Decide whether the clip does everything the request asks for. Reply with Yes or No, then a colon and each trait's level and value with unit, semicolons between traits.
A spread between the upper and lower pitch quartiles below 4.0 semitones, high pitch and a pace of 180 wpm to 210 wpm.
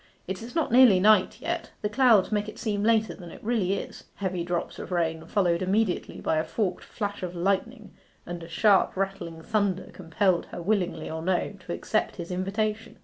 Yes: average, 3.5 semitones; high, 195 Hz; average, 190 wpm